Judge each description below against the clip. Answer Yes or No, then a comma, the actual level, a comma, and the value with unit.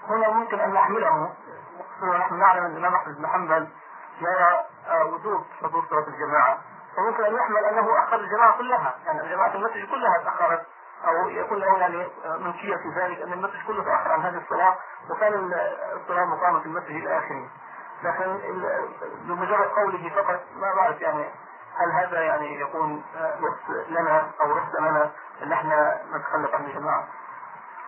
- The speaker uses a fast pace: Yes, fast, 150 wpm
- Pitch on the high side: Yes, high, 200 Hz